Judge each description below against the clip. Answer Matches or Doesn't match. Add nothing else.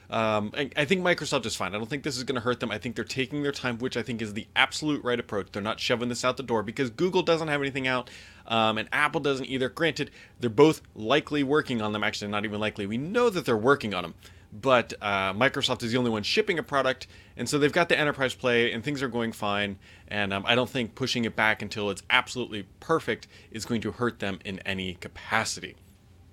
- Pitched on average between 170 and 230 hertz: Doesn't match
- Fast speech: Matches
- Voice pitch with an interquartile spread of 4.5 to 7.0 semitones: Matches